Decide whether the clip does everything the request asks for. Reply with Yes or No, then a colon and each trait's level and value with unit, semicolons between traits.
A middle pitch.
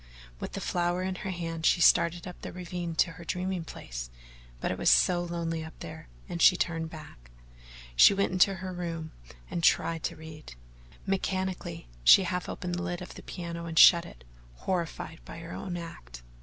Yes: medium, 170 Hz